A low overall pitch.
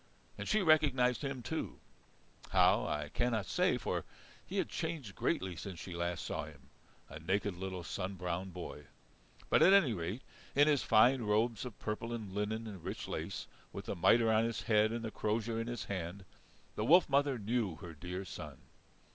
Yes: low, 105 Hz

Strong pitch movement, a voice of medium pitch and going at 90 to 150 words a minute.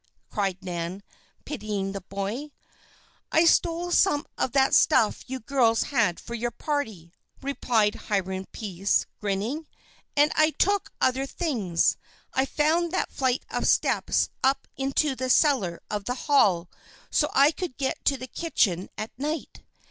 No: wide, 6.6 semitones; very high, 255 Hz; average, 145 wpm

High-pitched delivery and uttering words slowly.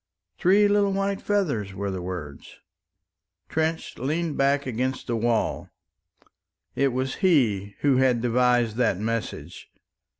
No: low, 130 Hz; slow, 125 wpm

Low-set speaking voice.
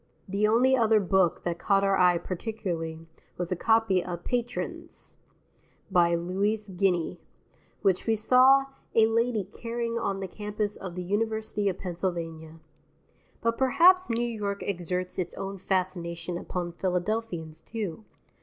No: high, 195 Hz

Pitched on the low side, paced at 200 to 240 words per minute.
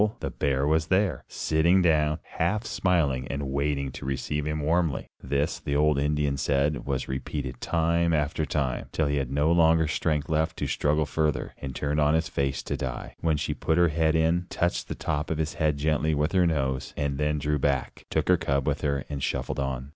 Yes: very low, 75 Hz; fast, 205 wpm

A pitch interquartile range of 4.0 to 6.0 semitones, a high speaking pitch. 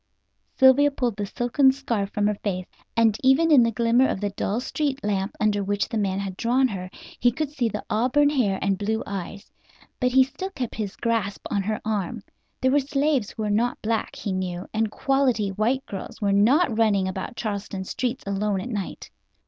Yes: average, 4.6 semitones; high, 220 Hz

